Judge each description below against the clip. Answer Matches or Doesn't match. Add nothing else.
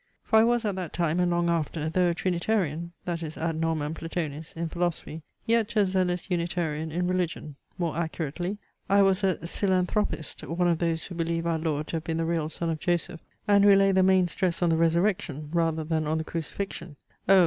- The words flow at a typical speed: Doesn't match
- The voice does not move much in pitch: Matches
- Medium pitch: Matches